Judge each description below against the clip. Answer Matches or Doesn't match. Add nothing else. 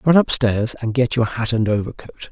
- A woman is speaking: Doesn't match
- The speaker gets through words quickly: Matches